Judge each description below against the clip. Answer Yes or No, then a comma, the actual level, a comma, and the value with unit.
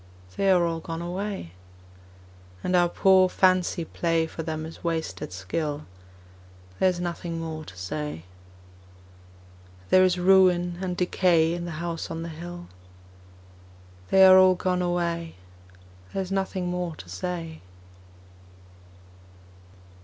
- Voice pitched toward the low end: No, medium, 175 Hz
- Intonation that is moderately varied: No, narrow, 2.0 semitones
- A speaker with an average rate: No, slow, 130 wpm